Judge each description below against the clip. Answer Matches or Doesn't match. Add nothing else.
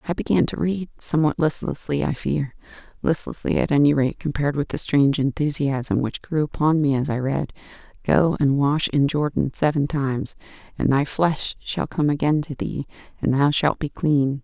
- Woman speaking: Matches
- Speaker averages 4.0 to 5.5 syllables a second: Matches